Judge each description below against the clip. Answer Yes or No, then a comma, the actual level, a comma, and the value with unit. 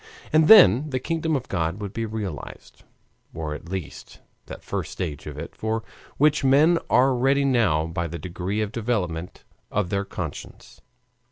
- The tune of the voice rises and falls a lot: Yes, wide, 7.7 semitones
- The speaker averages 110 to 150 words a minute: No, average, 165 wpm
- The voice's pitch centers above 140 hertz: No, low, 105 Hz